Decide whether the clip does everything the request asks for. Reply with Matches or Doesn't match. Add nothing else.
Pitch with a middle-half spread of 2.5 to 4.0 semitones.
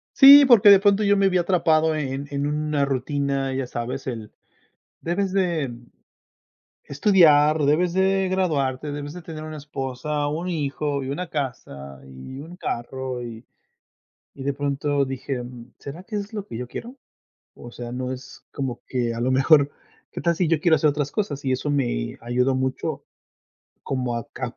Doesn't match